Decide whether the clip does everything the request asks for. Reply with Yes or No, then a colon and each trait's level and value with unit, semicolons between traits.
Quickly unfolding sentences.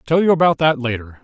Yes: fast, 245 wpm